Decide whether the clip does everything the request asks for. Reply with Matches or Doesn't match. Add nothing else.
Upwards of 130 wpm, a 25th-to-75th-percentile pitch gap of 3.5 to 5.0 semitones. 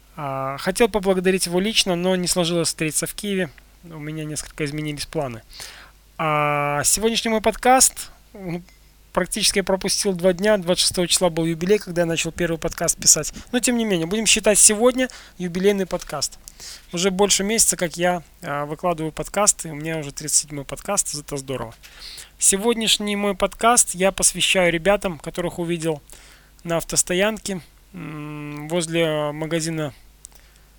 Matches